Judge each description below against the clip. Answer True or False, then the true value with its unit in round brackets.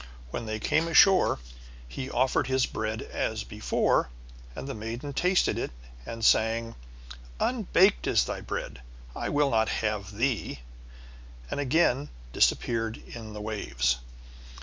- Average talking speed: False (130 wpm)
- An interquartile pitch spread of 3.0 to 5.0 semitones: True (4.6 semitones)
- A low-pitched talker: True (115 Hz)